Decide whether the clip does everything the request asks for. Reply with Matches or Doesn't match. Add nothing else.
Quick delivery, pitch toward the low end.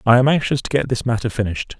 Matches